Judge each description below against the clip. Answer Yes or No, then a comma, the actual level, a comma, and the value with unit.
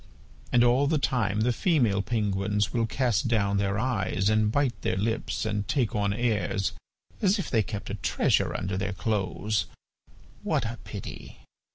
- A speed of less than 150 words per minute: No, average, 165 wpm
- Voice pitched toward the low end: Yes, low, 110 Hz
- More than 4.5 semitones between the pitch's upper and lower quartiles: No, average, 3.3 semitones